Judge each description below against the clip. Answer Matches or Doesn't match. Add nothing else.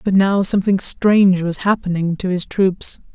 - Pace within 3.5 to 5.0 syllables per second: Matches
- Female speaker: Matches